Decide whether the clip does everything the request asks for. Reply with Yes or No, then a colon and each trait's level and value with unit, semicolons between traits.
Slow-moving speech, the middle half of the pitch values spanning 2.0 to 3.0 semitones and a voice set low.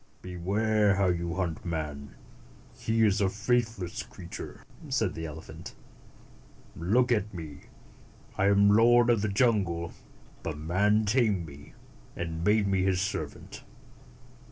No: slow, 130 wpm; average, 4.3 semitones; very low, 95 Hz